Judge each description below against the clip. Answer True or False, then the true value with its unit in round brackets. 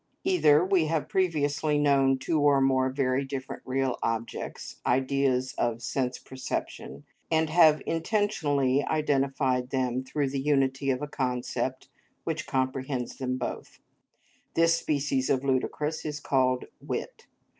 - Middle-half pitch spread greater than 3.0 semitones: False (2.4 semitones)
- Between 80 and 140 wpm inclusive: True (135 wpm)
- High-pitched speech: False (135 Hz)